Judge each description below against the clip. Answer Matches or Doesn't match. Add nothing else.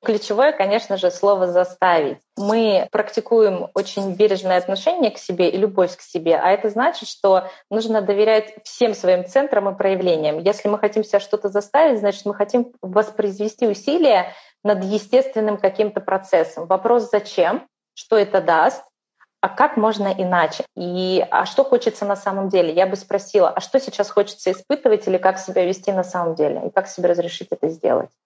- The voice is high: Matches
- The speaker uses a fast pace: Matches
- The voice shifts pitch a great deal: Doesn't match